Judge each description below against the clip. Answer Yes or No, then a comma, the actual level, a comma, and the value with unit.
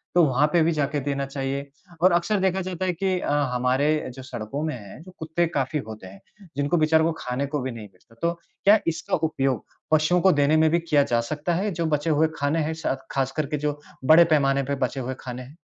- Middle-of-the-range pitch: Yes, medium, 150 Hz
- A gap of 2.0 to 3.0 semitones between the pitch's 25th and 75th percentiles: No, average, 3.7 semitones